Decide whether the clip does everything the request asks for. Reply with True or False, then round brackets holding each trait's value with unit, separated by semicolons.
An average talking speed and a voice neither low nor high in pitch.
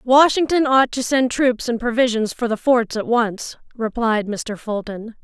False (170 wpm; 240 Hz)